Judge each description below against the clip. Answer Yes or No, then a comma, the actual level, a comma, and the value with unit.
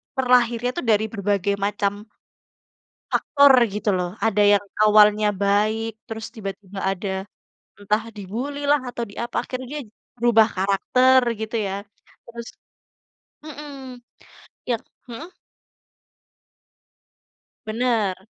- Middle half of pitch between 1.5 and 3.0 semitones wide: No, average, 3.4 semitones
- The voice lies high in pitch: Yes, high, 220 Hz